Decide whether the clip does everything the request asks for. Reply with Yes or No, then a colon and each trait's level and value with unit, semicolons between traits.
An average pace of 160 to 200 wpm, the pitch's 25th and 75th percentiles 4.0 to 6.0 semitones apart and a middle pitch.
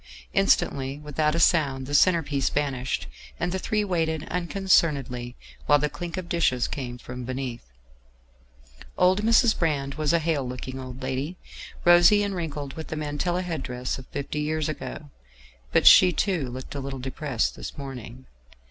Yes: average, 165 wpm; average, 4.4 semitones; medium, 145 Hz